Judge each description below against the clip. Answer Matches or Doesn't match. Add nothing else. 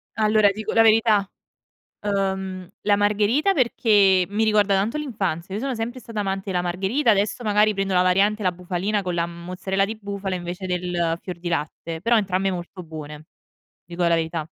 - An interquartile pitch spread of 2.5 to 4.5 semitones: Matches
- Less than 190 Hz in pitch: Doesn't match